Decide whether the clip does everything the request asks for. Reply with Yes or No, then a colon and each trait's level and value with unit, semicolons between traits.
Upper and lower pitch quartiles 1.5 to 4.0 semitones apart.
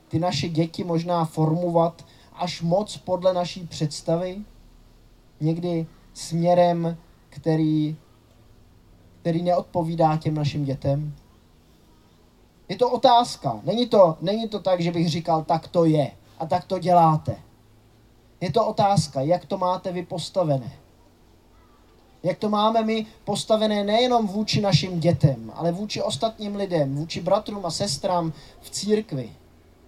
No: average, 5.3 semitones